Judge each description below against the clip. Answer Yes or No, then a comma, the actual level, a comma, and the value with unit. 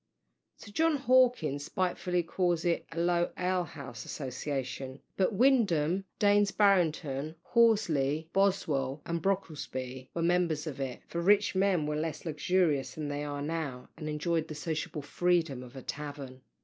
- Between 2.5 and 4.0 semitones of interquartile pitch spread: No, average, 4.4 semitones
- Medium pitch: Yes, medium, 160 Hz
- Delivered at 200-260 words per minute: No, average, 150 wpm